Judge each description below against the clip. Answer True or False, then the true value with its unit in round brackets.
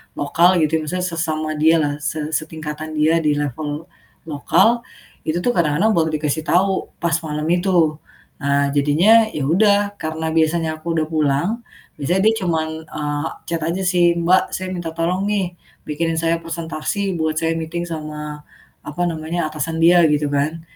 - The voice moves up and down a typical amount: False (2.2 semitones)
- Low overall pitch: False (160 Hz)